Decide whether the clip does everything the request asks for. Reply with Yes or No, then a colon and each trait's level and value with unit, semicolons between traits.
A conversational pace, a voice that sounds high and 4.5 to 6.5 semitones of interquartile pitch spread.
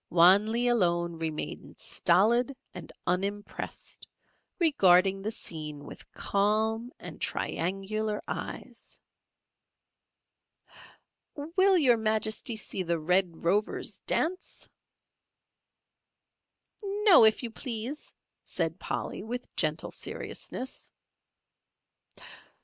No: slow, 85 wpm; high, 215 Hz; average, 5.1 semitones